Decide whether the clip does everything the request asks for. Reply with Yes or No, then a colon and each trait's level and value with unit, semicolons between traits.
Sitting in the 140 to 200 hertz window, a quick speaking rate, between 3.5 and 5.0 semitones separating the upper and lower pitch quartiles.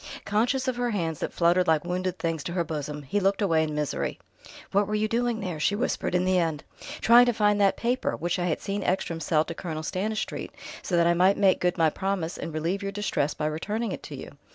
Yes: medium, 185 Hz; fast, 240 wpm; average, 4.1 semitones